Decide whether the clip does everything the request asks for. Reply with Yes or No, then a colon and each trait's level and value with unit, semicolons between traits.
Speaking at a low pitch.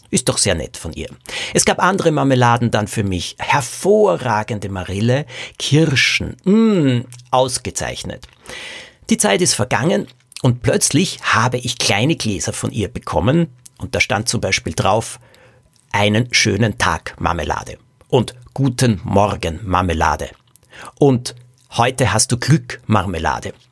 Yes: low, 125 Hz